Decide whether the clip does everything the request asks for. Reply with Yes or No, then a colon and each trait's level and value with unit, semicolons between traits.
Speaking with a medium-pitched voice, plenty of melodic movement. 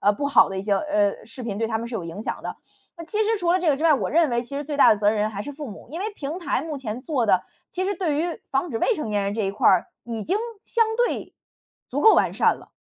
No: very high, 270 Hz; wide, 7.5 semitones